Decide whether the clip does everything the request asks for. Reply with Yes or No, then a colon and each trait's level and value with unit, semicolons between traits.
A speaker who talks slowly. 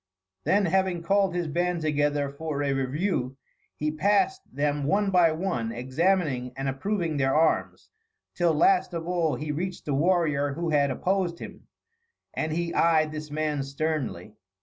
No: average, 155 wpm